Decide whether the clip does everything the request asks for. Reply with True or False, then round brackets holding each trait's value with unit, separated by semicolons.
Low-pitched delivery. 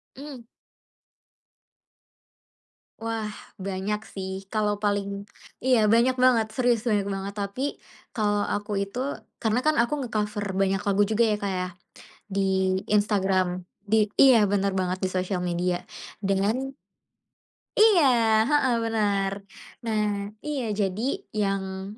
False (210 Hz)